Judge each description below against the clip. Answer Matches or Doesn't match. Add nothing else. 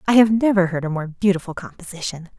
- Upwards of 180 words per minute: Matches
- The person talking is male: Doesn't match